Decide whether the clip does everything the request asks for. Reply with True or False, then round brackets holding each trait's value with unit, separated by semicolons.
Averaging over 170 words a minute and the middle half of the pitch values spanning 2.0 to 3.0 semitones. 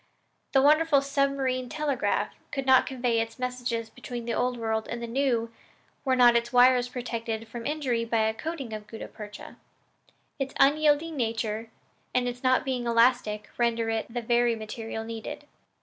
False (165 wpm; 2.5 semitones)